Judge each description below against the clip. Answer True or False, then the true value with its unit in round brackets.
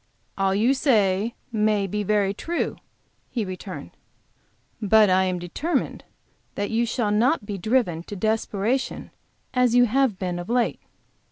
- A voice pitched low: False (210 Hz)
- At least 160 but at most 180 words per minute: False (145 wpm)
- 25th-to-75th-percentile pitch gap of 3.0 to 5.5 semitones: True (3.7 semitones)